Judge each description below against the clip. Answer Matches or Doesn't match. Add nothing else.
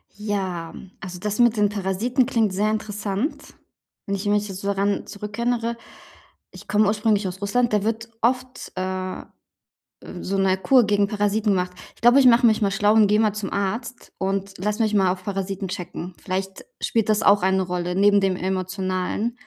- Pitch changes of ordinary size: Doesn't match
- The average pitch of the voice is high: Matches